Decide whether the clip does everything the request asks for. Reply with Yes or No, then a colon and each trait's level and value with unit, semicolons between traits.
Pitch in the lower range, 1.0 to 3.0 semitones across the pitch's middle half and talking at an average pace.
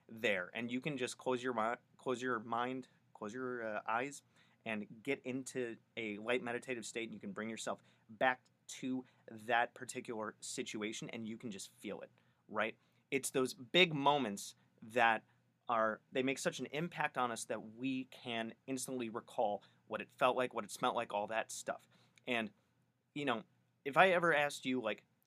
Yes: low, 125 Hz; average, 2.7 semitones; average, 180 wpm